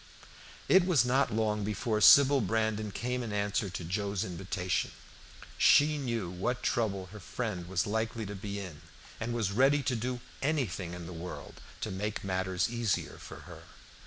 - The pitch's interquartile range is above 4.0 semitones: Yes, average, 4.4 semitones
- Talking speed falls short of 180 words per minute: Yes, average, 165 wpm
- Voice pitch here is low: Yes, low, 105 Hz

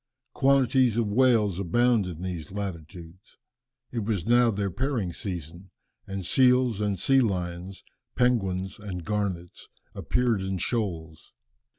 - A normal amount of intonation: Yes, average, 4.9 semitones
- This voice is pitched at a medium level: No, low, 100 Hz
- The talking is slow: Yes, slow, 120 wpm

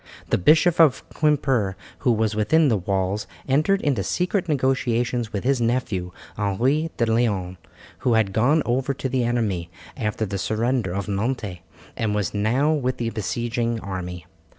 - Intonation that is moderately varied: Yes, average, 4.5 semitones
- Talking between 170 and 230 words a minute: No, average, 155 wpm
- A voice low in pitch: Yes, low, 115 Hz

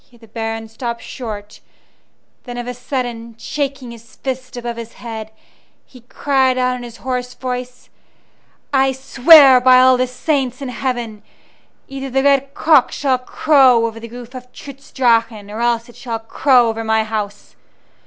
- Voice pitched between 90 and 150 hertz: No, very high, 250 Hz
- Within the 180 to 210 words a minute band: No, average, 165 wpm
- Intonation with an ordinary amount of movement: No, narrow, 2.3 semitones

